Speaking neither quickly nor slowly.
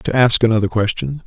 Yes: average, 190 wpm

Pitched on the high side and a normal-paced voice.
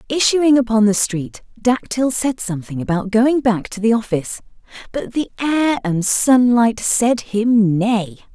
Yes: high, 225 Hz; average, 150 wpm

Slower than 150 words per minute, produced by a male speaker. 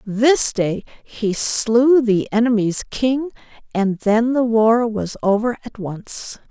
No: average, 140 wpm; female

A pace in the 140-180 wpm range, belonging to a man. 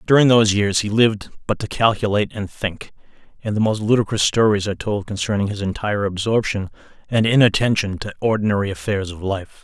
Yes: average, 175 wpm; male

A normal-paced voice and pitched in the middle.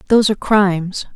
No: average, 155 wpm; high, 200 Hz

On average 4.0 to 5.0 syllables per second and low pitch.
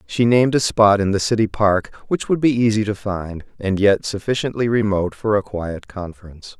No: 5.3 syllables/s; low, 105 Hz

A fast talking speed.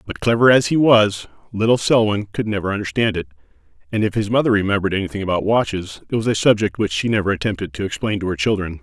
Yes: fast, 220 wpm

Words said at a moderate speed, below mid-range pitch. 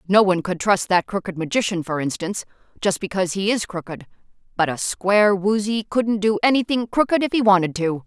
No: average, 195 wpm; high, 195 Hz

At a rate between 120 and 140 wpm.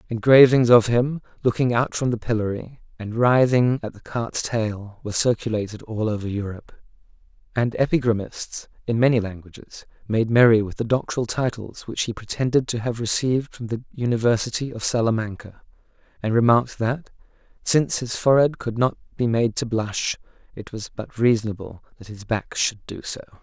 No: average, 160 wpm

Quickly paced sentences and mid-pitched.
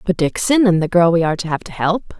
Yes: fast, 300 wpm; medium, 180 Hz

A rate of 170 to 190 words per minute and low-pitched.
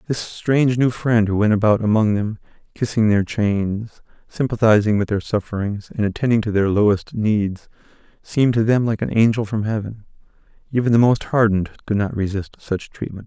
Yes: average, 175 wpm; low, 110 Hz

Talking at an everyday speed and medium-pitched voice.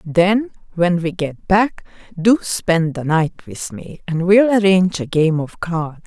Yes: average, 180 wpm; medium, 180 Hz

